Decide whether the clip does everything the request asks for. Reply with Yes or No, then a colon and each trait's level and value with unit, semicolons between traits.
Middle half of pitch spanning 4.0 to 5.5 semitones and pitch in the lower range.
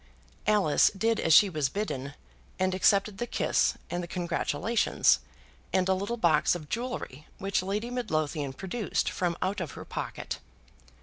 No: average, 4.8 semitones; medium, 185 Hz